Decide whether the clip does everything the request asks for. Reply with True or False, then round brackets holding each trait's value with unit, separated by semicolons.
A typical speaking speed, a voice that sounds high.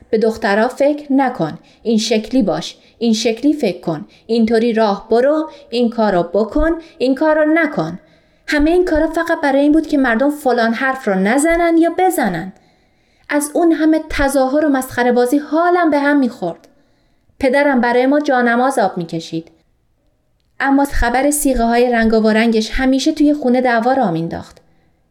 False (160 wpm; 260 Hz)